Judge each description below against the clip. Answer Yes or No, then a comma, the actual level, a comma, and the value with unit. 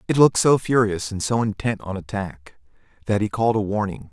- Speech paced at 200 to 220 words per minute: Yes, fast, 205 wpm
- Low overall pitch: Yes, low, 105 Hz